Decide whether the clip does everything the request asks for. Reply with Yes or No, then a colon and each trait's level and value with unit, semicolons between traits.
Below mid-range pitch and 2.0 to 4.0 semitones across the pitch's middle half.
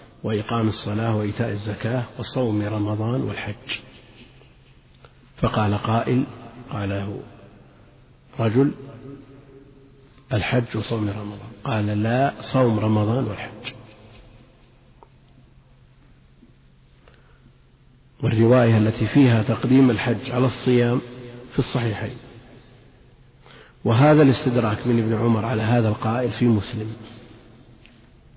Yes: low, 120 Hz; average, 2.7 semitones